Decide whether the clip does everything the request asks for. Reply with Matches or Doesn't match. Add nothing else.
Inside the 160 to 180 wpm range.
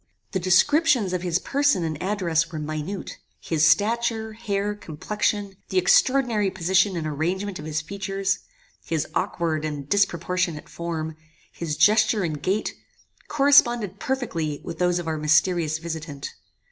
Doesn't match